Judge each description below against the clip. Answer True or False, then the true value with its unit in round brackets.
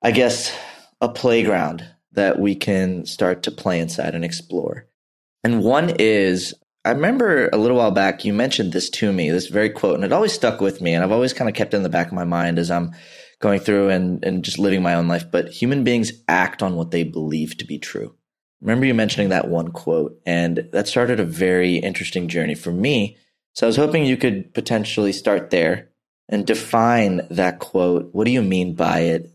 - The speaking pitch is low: True (95 Hz)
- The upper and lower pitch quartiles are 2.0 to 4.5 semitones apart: False (4.9 semitones)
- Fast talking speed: True (215 wpm)